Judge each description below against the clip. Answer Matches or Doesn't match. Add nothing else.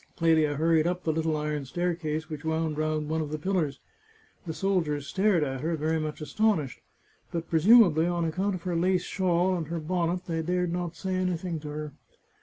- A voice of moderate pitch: Matches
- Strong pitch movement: Doesn't match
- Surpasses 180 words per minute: Matches